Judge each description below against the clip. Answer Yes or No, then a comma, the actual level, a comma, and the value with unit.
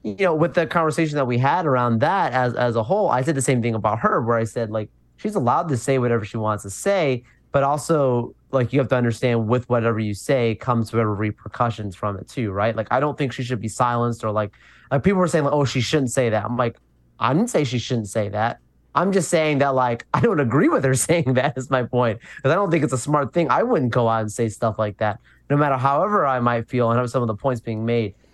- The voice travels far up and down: No, average, 3.5 semitones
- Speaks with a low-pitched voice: Yes, low, 125 Hz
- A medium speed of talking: No, fast, 270 wpm